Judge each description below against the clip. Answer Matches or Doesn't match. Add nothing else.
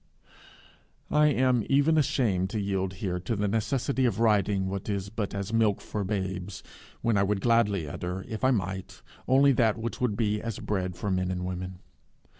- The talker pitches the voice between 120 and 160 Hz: Doesn't match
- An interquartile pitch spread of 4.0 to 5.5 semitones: Doesn't match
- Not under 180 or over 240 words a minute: Matches